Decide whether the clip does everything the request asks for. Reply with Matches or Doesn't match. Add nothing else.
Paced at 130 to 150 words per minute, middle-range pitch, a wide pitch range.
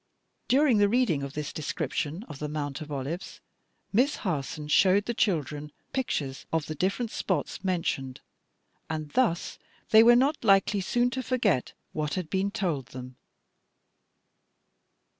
Matches